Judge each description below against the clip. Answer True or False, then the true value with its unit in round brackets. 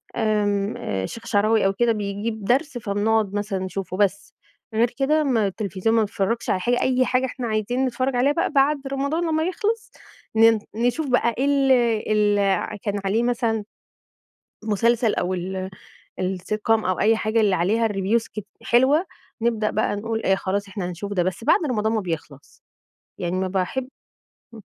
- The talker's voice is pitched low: False (220 Hz)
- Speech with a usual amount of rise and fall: True (3.7 semitones)